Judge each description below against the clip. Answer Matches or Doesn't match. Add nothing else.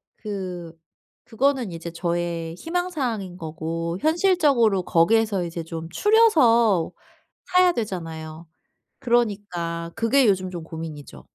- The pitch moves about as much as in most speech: Doesn't match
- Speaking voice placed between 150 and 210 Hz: Matches